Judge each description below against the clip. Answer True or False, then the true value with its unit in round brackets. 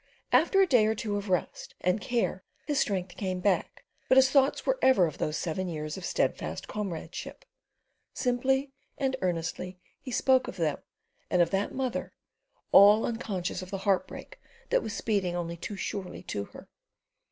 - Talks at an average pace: True (170 wpm)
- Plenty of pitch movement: True (6.0 semitones)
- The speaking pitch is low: False (200 Hz)